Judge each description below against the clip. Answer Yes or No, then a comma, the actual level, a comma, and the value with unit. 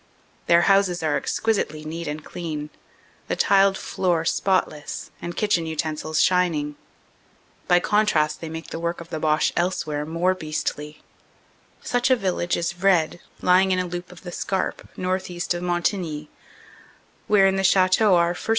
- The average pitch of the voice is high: No, medium, 175 Hz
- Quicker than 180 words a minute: No, average, 160 wpm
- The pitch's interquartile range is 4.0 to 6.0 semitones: No, average, 2.9 semitones